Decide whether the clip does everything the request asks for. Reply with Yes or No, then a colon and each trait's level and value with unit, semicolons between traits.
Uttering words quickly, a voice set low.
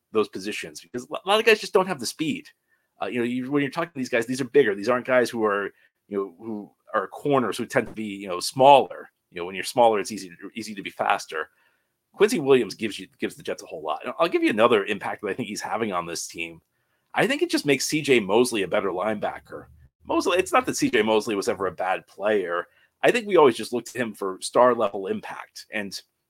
Yes: fast, 255 wpm; low, 120 Hz